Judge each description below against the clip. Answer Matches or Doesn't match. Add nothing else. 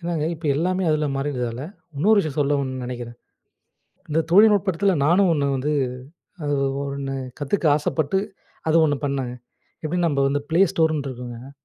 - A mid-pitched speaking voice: Matches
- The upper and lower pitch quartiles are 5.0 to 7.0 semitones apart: Doesn't match